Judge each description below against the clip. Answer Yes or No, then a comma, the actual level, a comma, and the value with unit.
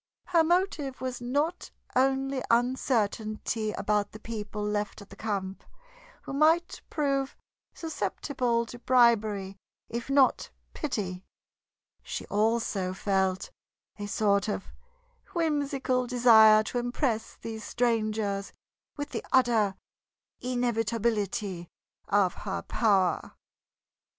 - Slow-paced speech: Yes, slow, 100 wpm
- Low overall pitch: No, high, 230 Hz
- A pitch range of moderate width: Yes, average, 4.0 semitones